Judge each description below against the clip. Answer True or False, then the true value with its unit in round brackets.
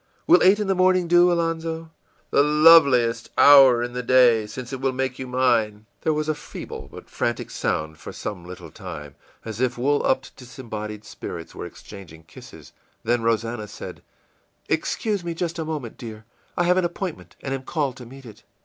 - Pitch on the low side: True (130 Hz)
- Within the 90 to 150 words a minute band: False (185 wpm)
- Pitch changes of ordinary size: False (6.2 semitones)